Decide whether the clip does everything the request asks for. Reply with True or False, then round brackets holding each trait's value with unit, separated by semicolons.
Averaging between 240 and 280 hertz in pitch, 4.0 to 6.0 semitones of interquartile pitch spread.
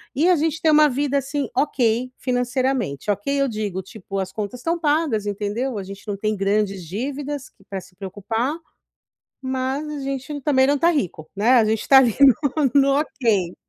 True (255 Hz; 5.5 semitones)